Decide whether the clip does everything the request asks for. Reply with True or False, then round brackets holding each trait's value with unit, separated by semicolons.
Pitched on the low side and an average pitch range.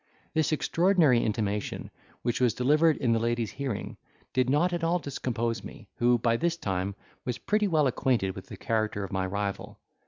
False (120 Hz; 5.9 semitones)